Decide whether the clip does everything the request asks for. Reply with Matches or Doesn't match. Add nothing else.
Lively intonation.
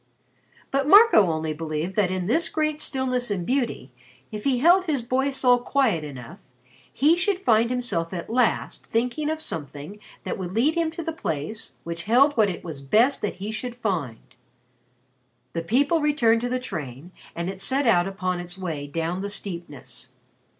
Matches